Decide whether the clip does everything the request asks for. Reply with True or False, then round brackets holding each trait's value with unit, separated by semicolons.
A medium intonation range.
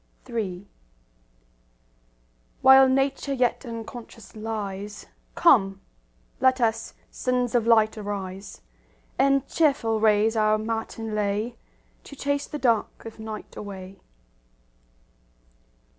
True (3.2 semitones)